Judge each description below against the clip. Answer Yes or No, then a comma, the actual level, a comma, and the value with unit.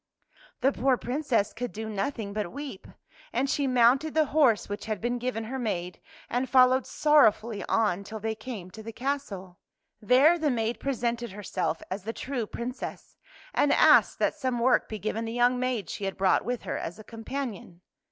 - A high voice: Yes, high, 235 Hz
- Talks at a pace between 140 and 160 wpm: No, average, 190 wpm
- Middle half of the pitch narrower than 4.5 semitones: Yes, average, 3.5 semitones